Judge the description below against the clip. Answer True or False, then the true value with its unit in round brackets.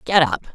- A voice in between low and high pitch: True (155 Hz)